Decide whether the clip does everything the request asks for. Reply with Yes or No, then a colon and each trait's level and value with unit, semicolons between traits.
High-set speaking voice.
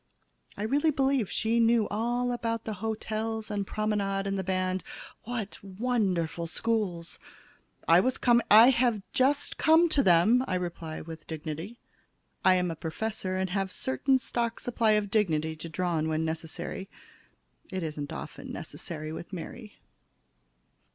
Yes: high, 200 Hz